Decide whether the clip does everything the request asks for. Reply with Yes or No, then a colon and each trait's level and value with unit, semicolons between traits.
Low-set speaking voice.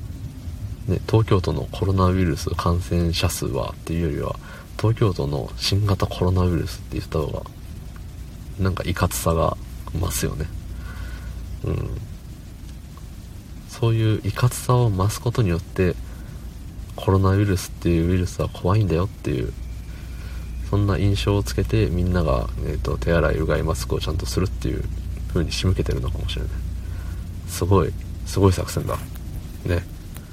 Yes: very low, 90 Hz